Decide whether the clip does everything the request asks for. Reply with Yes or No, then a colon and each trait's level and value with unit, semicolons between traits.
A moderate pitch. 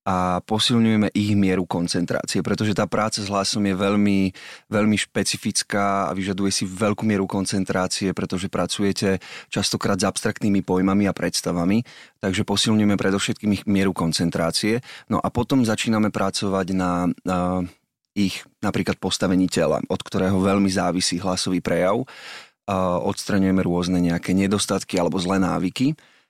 No: very low, 95 Hz